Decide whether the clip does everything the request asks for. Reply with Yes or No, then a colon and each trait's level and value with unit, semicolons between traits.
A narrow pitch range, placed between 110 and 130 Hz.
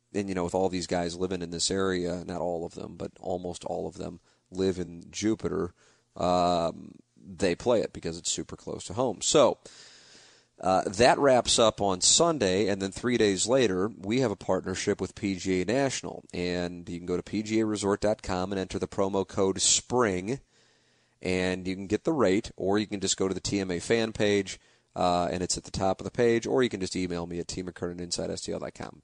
No: narrow, 2.3 semitones; very low, 95 Hz